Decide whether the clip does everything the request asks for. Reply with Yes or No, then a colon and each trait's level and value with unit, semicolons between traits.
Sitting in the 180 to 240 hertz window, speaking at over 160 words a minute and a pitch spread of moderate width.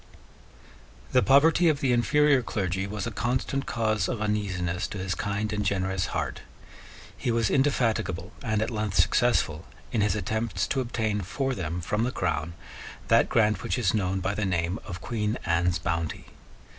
No: low, 105 Hz; average, 170 wpm; average, 4.2 semitones